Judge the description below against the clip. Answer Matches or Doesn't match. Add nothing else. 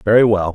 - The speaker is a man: Matches